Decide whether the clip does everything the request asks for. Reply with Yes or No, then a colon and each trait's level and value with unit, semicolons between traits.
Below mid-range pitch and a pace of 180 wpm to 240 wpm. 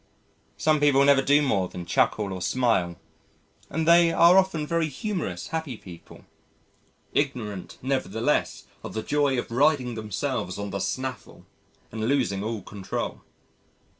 No: low, 130 Hz; slow, 135 wpm